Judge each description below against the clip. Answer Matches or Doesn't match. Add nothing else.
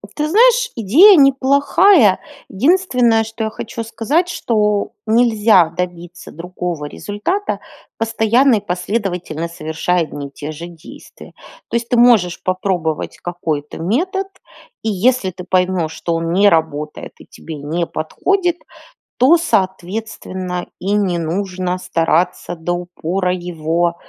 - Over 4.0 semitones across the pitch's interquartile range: Matches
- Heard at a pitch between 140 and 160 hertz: Doesn't match